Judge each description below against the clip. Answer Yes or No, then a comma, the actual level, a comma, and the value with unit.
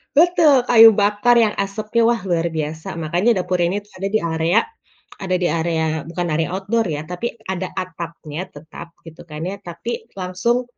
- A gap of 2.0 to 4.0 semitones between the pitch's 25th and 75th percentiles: No, average, 4.6 semitones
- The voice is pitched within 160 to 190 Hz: Yes, medium, 185 Hz